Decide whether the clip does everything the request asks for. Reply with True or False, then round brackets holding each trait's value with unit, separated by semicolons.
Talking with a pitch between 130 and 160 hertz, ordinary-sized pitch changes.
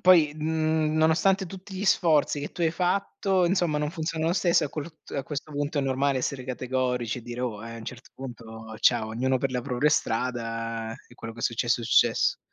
True (140 Hz; 5.0 semitones)